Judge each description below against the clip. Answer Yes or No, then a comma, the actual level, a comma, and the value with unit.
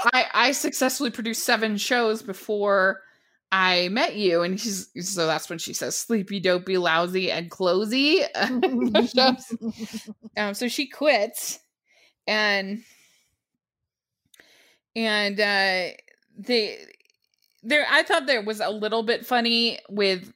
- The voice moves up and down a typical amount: Yes, average, 4.1 semitones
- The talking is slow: Yes, slow, 120 wpm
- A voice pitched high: Yes, high, 220 Hz